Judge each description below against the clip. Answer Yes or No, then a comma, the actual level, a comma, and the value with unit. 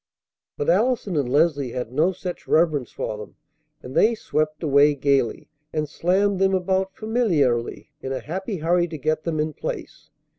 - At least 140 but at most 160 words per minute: No, average, 170 wpm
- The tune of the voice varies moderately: Yes, average, 5.0 semitones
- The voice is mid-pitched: Yes, medium, 155 Hz